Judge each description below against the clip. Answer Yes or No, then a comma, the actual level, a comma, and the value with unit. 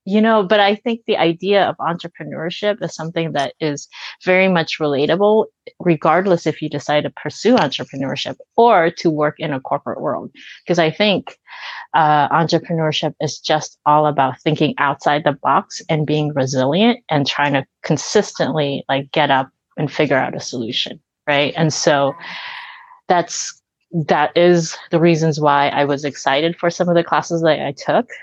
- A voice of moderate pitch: Yes, medium, 160 Hz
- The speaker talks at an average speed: Yes, average, 165 wpm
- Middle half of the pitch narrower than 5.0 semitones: Yes, average, 3.8 semitones